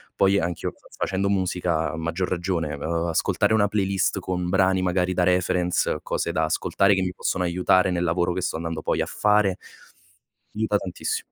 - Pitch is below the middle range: Yes, very low, 90 Hz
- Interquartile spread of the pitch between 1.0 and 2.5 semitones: Yes, narrow, 1.8 semitones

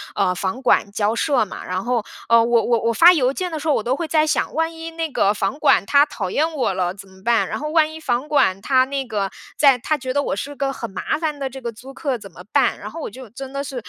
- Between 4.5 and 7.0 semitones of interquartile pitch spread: Yes, average, 5.1 semitones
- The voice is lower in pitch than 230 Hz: No, very high, 260 Hz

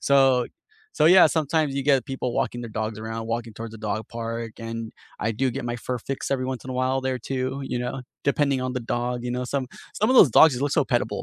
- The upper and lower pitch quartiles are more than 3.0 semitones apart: No, average, 2.7 semitones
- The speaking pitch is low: Yes, low, 125 Hz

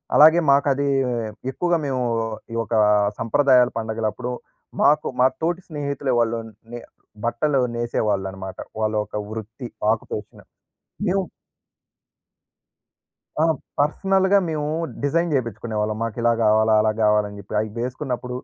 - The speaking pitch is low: Yes, low, 125 Hz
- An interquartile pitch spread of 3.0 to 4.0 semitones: No, average, 4.9 semitones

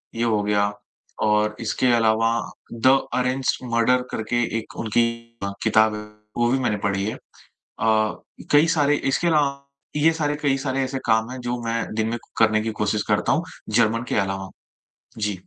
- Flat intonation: No, average, 3.5 semitones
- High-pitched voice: No, low, 115 Hz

